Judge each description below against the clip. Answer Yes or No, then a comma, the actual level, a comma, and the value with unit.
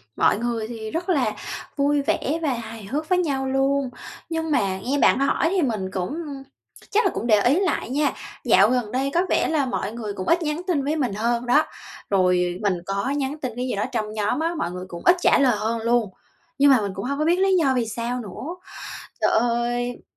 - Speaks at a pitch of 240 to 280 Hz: Yes, very high, 250 Hz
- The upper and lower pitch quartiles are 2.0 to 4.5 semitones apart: No, average, 5.2 semitones